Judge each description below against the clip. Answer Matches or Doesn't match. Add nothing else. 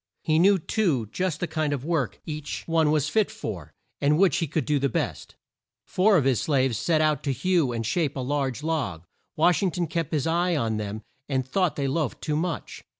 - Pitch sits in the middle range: Matches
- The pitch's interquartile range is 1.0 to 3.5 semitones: Doesn't match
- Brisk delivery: Matches